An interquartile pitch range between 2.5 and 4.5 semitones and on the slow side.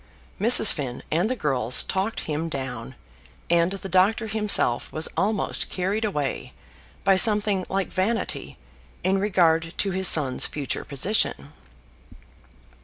No: wide, 5.6 semitones; slow, 125 wpm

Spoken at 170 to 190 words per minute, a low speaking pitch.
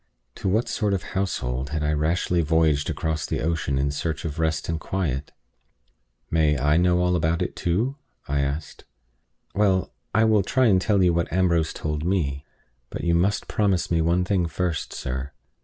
Yes: average, 180 wpm; very low, 85 Hz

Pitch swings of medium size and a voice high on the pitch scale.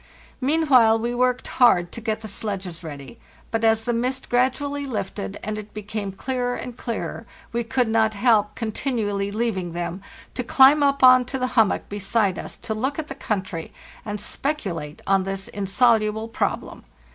Yes: average, 3.9 semitones; high, 225 Hz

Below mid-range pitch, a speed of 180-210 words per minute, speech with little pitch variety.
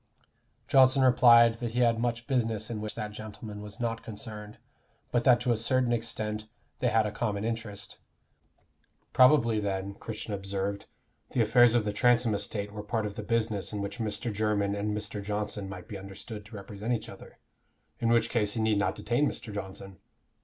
Yes: low, 110 Hz; average, 185 wpm; narrow, 2.2 semitones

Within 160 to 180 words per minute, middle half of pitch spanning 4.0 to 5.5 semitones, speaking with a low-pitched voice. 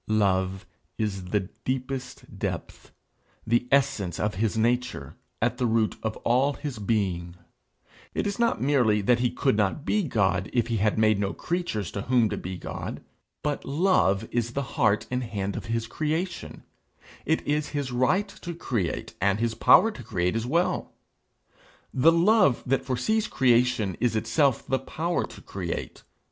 Yes: average, 165 wpm; average, 5.1 semitones; low, 120 Hz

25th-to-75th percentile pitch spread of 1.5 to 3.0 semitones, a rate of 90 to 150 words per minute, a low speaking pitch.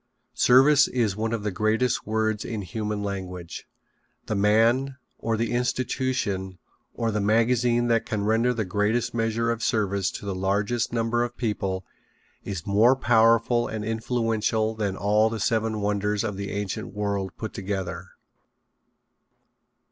Yes: narrow, 2.4 semitones; average, 145 wpm; low, 110 Hz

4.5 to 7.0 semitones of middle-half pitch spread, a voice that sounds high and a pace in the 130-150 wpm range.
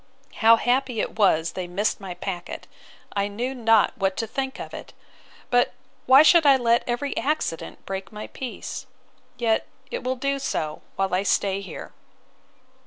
No: average, 5.1 semitones; high, 225 Hz; average, 160 wpm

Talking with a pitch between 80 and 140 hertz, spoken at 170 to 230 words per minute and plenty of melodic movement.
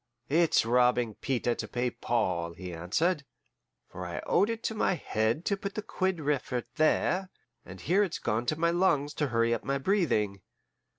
Yes: low, 135 Hz; average, 180 wpm; wide, 7.4 semitones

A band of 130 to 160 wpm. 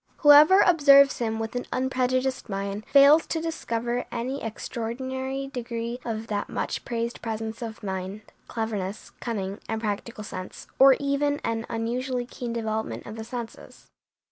Yes: average, 145 wpm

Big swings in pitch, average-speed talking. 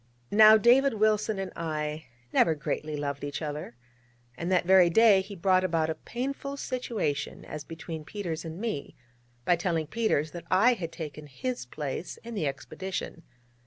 Yes: wide, 5.7 semitones; average, 165 wpm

